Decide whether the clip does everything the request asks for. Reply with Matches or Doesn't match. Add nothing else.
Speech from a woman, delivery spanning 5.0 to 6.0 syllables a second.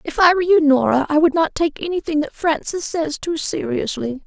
Matches